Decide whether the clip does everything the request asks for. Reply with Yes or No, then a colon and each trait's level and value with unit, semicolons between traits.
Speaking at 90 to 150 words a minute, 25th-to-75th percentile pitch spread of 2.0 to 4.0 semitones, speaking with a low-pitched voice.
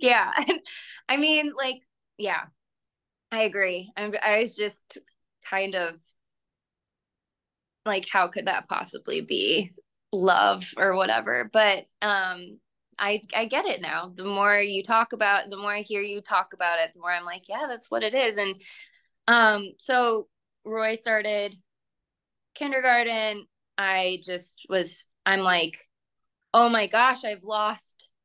No: average, 140 wpm; average, 3.1 semitones; high, 210 Hz